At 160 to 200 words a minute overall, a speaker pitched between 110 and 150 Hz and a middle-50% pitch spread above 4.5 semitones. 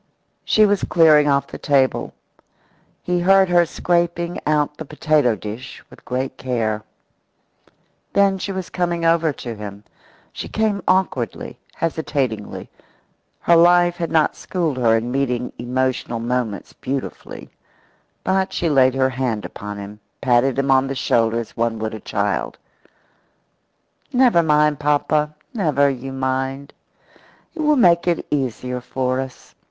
No: average, 140 wpm; medium, 140 Hz; wide, 5.5 semitones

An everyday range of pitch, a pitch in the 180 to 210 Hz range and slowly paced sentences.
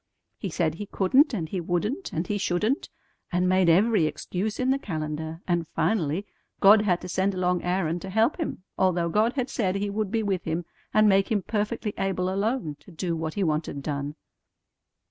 No: average, 3.9 semitones; high, 190 Hz; average, 195 wpm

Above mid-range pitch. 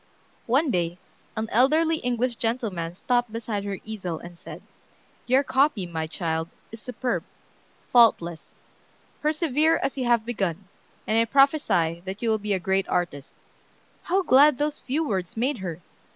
Yes: high, 225 Hz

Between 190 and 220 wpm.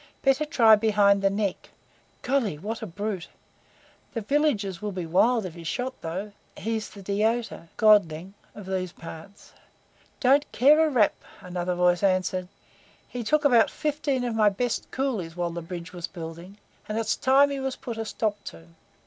No: average, 170 wpm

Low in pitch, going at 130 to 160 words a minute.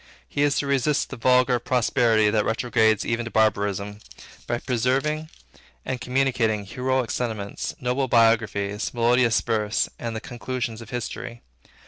Yes: low, 120 Hz; slow, 135 wpm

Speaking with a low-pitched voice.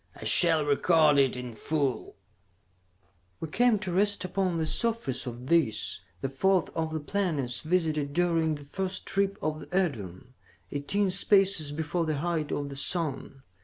No: medium, 160 Hz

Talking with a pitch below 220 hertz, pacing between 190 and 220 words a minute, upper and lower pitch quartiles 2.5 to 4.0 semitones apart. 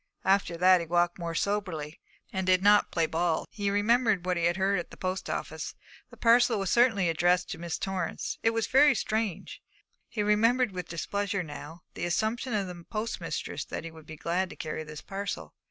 Yes: medium, 185 Hz; average, 200 wpm; average, 3.6 semitones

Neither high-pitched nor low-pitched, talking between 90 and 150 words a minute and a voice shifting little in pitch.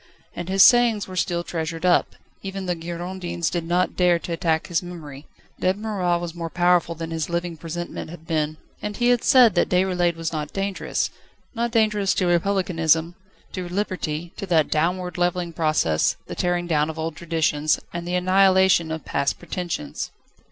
No: medium, 175 Hz; average, 175 wpm; narrow, 2.2 semitones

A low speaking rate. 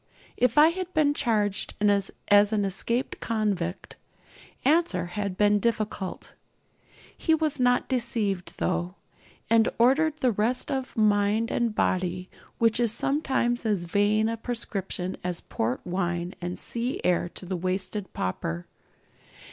Yes: slow, 130 wpm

